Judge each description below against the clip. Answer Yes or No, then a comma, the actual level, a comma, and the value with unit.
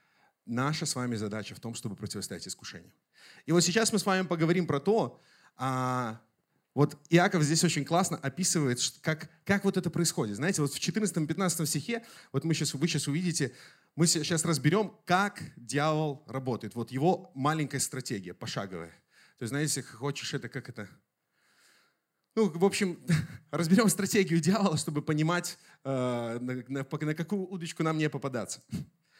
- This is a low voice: No, medium, 155 Hz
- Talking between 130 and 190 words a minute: Yes, average, 150 wpm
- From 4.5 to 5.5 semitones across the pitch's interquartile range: Yes, average, 4.9 semitones